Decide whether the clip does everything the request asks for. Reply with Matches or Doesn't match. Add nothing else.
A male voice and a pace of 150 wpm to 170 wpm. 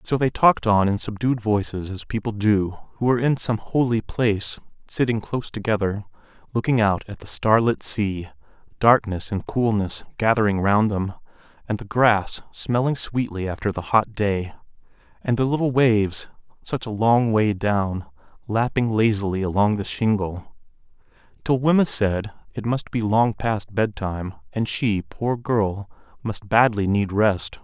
Matches